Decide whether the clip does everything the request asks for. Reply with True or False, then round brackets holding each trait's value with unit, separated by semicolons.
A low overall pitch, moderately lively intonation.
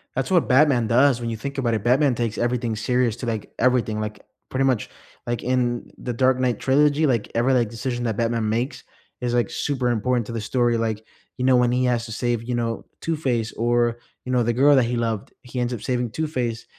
False (120 Hz; 1.7 semitones)